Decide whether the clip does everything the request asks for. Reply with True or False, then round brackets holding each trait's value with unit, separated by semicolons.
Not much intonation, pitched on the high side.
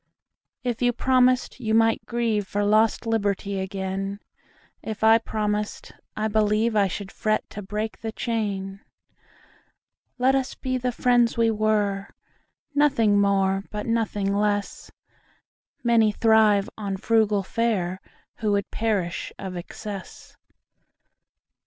True (2.3 semitones; 215 Hz)